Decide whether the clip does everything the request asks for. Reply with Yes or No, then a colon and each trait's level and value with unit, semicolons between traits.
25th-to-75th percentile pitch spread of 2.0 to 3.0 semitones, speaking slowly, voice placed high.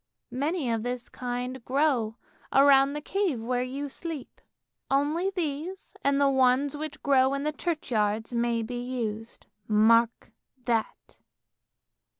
No: average, 3.5 semitones; slow, 130 wpm; very high, 260 Hz